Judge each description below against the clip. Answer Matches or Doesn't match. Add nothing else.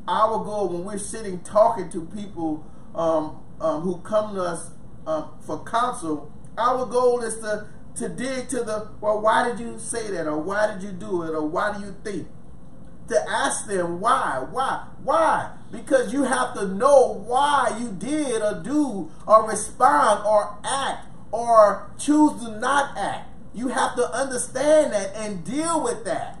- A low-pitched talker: Doesn't match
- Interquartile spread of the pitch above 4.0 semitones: Matches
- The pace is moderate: Matches